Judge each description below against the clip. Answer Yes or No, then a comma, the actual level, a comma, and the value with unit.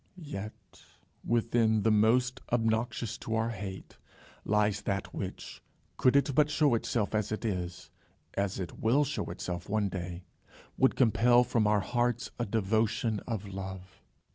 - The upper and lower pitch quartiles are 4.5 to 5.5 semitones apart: No, average, 3.3 semitones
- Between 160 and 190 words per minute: No, average, 150 wpm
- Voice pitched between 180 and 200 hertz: No, low, 110 Hz